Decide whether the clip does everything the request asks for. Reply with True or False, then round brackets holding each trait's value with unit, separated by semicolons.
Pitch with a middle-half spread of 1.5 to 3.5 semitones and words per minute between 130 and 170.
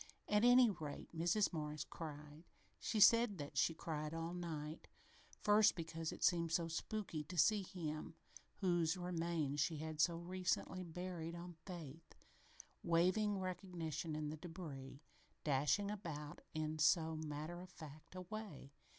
True (2.9 semitones; 145 wpm)